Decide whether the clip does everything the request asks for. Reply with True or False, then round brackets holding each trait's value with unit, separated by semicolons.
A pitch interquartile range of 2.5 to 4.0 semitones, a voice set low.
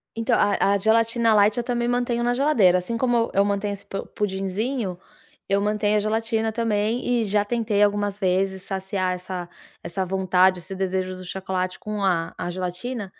False (3.1 semitones; 205 Hz)